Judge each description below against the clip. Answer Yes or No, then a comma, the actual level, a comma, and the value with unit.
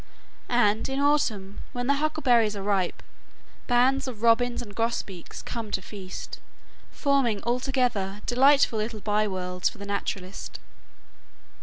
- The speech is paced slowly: Yes, slow, 125 wpm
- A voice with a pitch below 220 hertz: No, high, 230 Hz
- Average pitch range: Yes, average, 3.9 semitones